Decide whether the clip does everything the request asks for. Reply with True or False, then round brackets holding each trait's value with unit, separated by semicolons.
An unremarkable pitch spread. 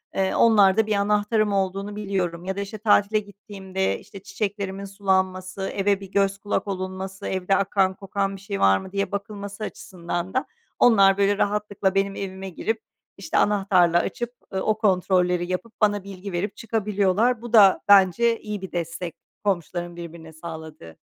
False (1.7 semitones)